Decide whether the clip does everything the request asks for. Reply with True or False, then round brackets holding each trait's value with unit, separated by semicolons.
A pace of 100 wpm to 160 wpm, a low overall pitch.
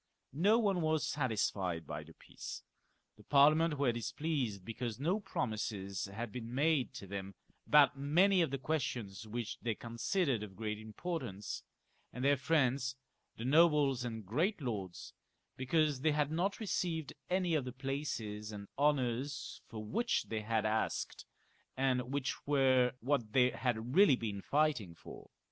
True (150 wpm; 130 Hz)